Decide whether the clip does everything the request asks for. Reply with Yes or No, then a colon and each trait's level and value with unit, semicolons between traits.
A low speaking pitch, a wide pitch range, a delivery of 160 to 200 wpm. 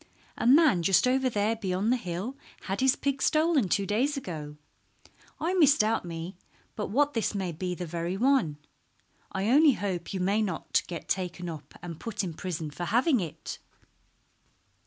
No: high, 200 Hz; wide, 6.6 semitones; average, 170 wpm